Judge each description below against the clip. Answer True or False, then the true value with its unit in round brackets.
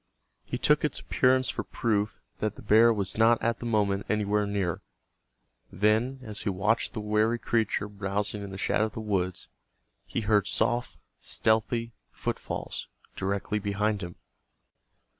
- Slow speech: False (150 wpm)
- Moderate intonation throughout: False (1.9 semitones)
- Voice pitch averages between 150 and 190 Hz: False (105 Hz)